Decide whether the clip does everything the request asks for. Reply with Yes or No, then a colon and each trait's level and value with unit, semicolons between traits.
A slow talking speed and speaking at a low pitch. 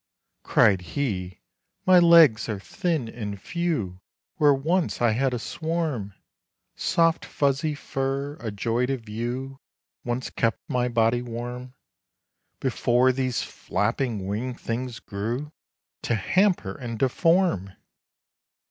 Yes: slow, 95 wpm; low, 125 Hz